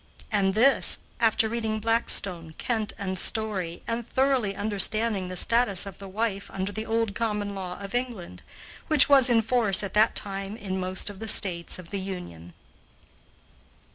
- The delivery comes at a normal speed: Yes, average, 165 wpm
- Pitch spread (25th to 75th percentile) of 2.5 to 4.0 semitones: Yes, average, 3.1 semitones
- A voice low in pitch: No, high, 205 Hz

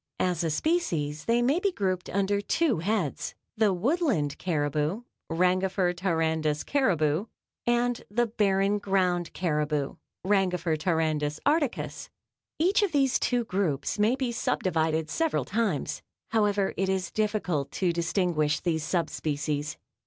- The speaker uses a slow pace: Yes, slow, 130 wpm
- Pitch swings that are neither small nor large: No, wide, 5.7 semitones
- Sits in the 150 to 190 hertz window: Yes, medium, 185 Hz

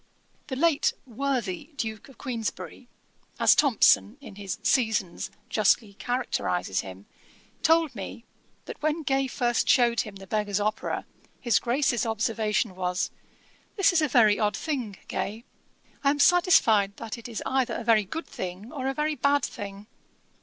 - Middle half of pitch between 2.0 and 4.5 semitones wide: No, average, 5.1 semitones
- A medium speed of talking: Yes, average, 155 wpm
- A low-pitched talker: No, high, 235 Hz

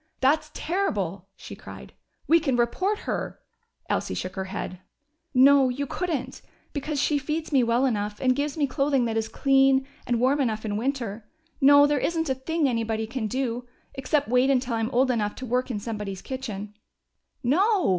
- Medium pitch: No, very high, 260 Hz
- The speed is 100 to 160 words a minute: No, average, 180 wpm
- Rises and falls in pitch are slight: No, average, 4.1 semitones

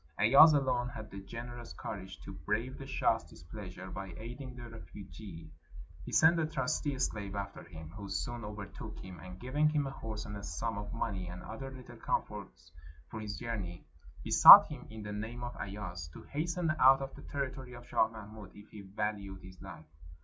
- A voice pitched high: No, low, 110 Hz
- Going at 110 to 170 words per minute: No, average, 190 wpm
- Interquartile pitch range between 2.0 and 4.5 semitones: Yes, average, 4.1 semitones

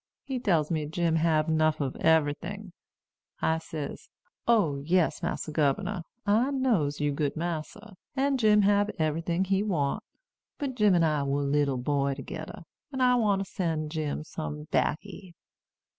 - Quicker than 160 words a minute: No, average, 155 wpm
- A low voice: No, medium, 165 Hz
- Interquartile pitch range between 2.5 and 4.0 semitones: No, average, 5.3 semitones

